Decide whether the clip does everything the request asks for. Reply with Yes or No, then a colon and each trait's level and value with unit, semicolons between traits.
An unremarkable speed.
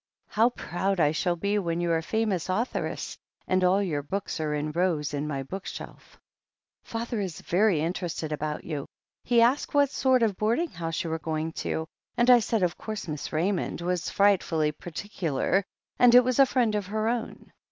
Yes: average, 190 wpm